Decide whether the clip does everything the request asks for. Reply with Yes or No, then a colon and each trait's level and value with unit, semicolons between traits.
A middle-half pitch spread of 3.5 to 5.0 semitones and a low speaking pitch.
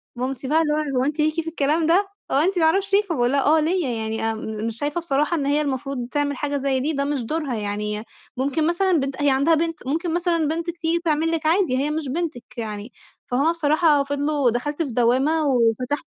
No: average, 3.9 semitones; very high, 290 Hz